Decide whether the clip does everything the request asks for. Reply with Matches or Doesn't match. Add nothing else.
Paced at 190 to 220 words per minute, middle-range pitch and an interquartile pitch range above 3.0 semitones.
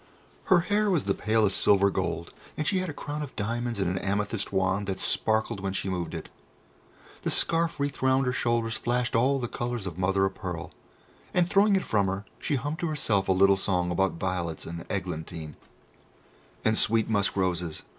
Doesn't match